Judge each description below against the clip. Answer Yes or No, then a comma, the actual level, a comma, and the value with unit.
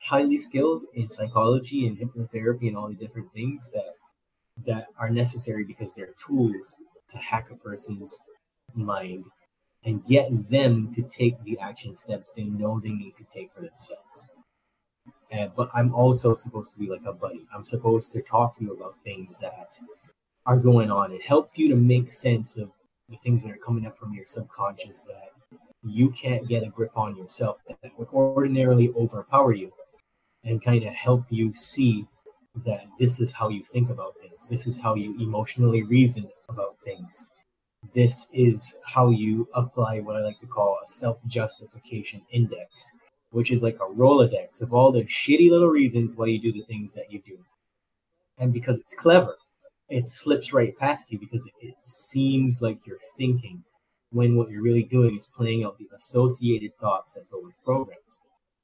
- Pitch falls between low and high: No, low, 120 Hz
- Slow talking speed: No, average, 180 wpm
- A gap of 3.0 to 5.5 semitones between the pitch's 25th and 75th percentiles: No, narrow, 2.5 semitones